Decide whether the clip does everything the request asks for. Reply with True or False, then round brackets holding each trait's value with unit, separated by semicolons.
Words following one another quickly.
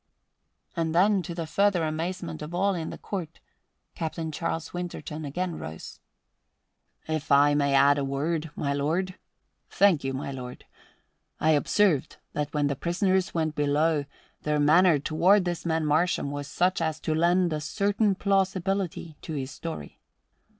False (155 wpm)